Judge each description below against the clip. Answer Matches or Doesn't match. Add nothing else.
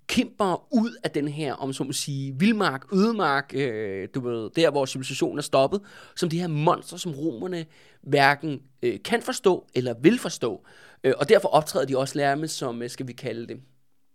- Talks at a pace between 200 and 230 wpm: Doesn't match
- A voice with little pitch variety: Doesn't match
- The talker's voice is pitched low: Doesn't match